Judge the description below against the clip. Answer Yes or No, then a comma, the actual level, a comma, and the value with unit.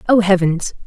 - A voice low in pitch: No, high, 190 Hz